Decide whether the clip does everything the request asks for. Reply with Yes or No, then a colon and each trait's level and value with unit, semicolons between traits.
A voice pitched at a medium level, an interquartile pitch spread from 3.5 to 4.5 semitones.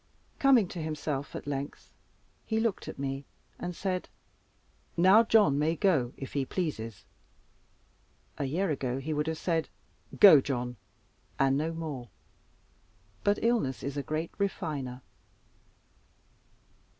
No: medium, 155 Hz; average, 5.1 semitones